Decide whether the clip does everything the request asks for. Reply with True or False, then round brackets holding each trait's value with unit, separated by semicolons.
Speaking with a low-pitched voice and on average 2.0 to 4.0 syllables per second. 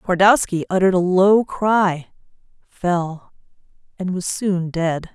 False (185 Hz; 3.7 syllables/s)